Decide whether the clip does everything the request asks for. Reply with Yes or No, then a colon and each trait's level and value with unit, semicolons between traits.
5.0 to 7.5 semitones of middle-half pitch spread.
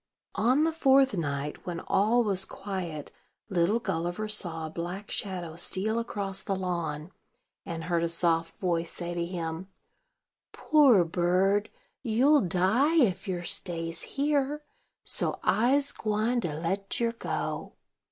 Yes: average, 5.3 semitones